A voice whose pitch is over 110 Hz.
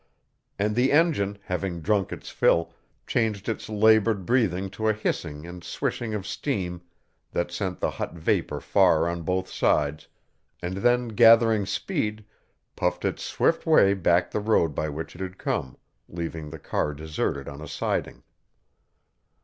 No: very low, 95 Hz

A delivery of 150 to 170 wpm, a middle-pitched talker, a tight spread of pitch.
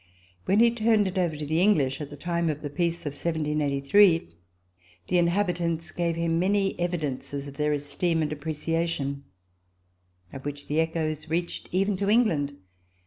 No: average, 165 wpm; medium, 165 Hz; average, 3.3 semitones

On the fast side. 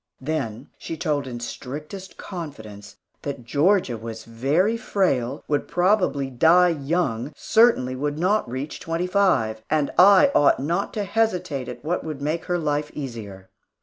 No: average, 150 wpm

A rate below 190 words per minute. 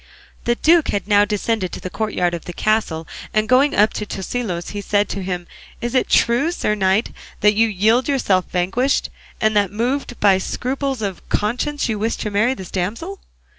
No: average, 195 wpm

